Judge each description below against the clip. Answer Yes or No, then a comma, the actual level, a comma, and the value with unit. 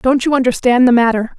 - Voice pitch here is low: No, very high, 250 Hz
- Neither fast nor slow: No, fast, 215 wpm